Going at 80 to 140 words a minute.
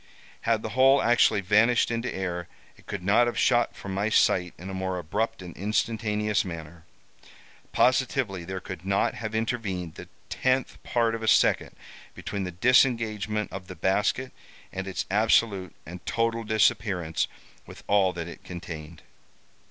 No: average, 155 wpm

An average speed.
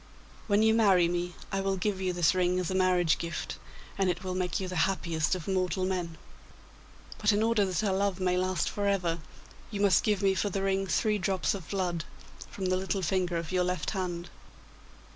No: fast, 210 wpm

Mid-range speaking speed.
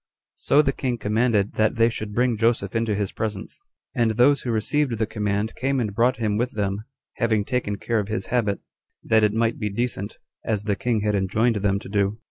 No: fast, 210 wpm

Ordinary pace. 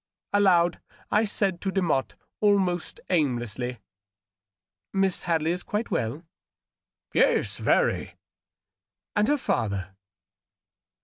No: slow, 110 wpm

